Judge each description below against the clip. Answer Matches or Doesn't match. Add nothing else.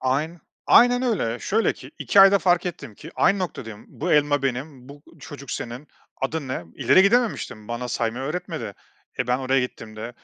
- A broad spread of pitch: Matches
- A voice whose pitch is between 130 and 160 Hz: Matches